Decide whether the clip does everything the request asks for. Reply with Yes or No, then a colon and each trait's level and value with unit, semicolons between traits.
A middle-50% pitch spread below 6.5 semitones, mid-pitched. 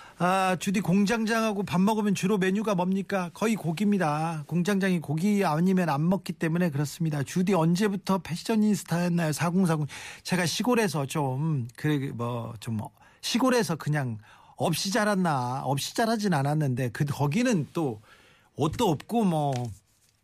Yes: wide, 5.4 semitones; medium, 175 Hz